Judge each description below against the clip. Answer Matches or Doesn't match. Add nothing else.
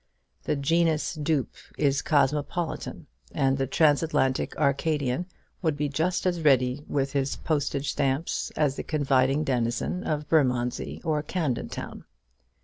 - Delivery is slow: Matches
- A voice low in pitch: Doesn't match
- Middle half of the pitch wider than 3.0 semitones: Doesn't match